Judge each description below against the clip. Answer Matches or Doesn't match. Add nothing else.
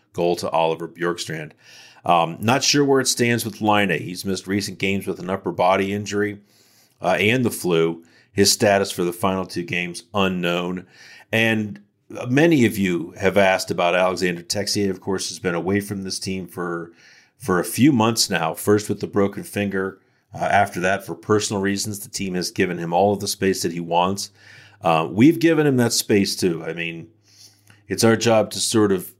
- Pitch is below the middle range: Matches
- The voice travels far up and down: Doesn't match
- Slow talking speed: Doesn't match